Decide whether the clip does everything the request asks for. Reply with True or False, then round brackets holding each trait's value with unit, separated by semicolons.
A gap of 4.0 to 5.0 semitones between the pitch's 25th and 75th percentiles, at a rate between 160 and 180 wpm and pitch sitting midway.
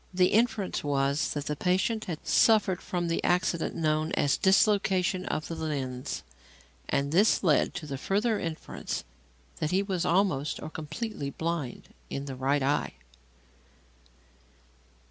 False (4.7 semitones; 140 wpm; 165 Hz)